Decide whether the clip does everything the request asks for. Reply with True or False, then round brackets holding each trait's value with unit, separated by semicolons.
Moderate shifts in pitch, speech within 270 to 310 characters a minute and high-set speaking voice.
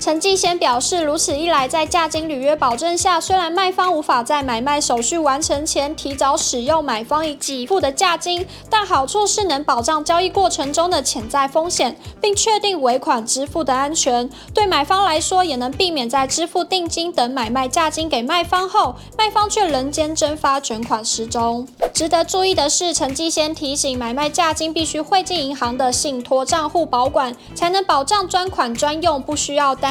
True (4.2 semitones; 290 characters per minute; 310 Hz)